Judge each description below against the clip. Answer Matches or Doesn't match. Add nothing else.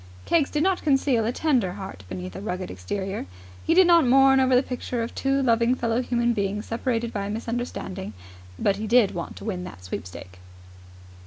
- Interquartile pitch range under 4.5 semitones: Doesn't match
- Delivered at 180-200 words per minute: Matches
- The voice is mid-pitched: Doesn't match